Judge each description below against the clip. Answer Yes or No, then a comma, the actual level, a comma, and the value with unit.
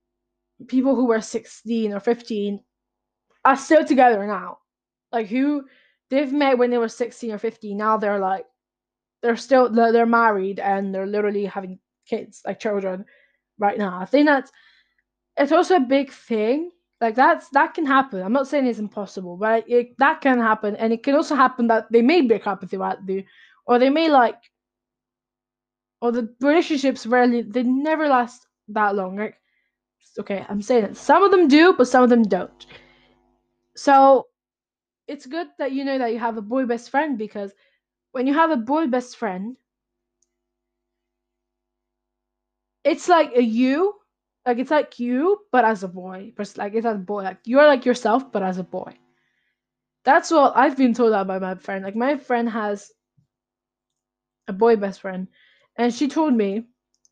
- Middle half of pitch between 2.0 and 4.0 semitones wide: No, average, 4.9 semitones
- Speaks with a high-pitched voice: Yes, high, 235 Hz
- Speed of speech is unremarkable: Yes, average, 175 wpm